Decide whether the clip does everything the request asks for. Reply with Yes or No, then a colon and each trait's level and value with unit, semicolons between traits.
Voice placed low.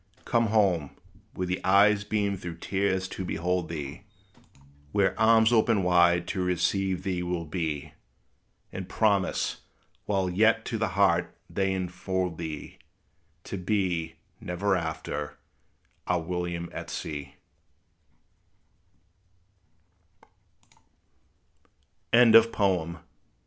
Yes: very low, 90 Hz